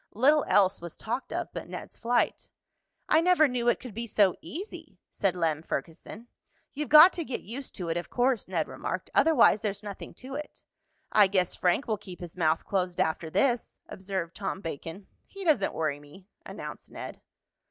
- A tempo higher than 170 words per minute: Yes, average, 185 wpm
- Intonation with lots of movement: Yes, wide, 6.6 semitones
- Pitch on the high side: Yes, high, 205 Hz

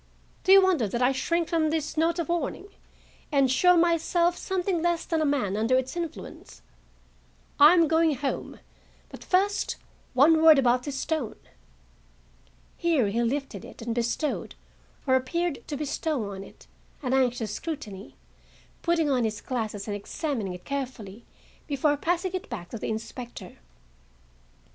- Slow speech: No, average, 155 wpm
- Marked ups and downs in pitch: Yes, wide, 5.9 semitones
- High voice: Yes, very high, 285 Hz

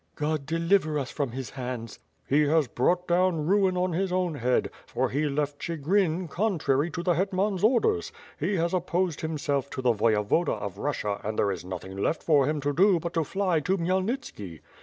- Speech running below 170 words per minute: No, average, 190 wpm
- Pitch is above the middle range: No, medium, 155 Hz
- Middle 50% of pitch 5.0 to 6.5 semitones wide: Yes, average, 5.3 semitones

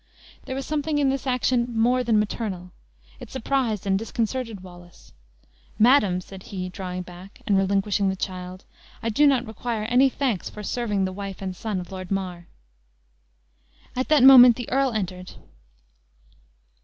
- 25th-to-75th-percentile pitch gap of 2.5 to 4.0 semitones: No, average, 5.0 semitones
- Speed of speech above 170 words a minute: No, average, 155 wpm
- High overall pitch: Yes, high, 210 Hz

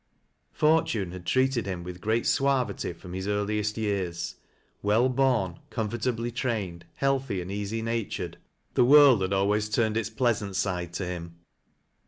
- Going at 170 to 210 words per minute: No, average, 145 wpm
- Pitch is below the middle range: Yes, low, 105 Hz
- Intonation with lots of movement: No, average, 4.2 semitones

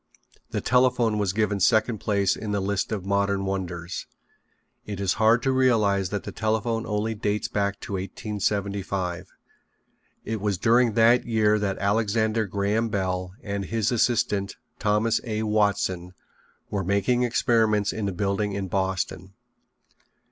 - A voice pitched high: No, low, 105 Hz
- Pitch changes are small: Yes, narrow, 2.2 semitones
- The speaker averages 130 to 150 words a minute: Yes, average, 140 wpm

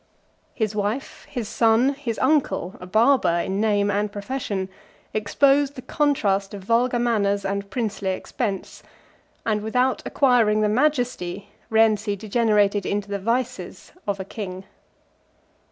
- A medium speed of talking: No, slow, 130 wpm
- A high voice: Yes, high, 215 Hz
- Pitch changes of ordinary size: Yes, average, 3.5 semitones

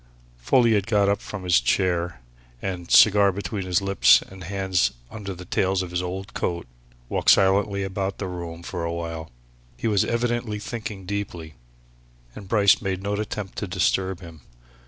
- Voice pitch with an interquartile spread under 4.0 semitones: Yes, narrow, 2.4 semitones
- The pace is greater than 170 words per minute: No, average, 165 wpm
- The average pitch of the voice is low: Yes, very low, 95 Hz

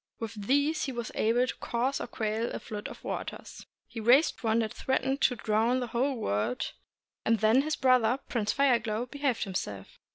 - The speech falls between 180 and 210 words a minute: Yes, average, 195 wpm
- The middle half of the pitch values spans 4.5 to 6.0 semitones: No, average, 3.2 semitones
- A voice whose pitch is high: Yes, high, 235 Hz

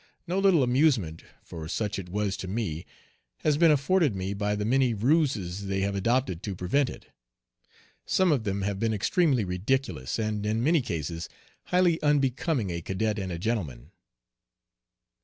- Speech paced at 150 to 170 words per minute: Yes, average, 160 wpm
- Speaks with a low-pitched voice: Yes, low, 105 Hz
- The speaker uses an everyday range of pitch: No, wide, 6.6 semitones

